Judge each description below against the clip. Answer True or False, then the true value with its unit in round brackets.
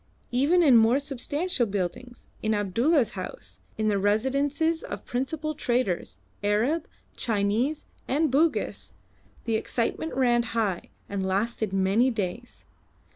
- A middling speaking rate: False (120 wpm)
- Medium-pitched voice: False (240 Hz)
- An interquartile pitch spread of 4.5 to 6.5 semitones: True (5.4 semitones)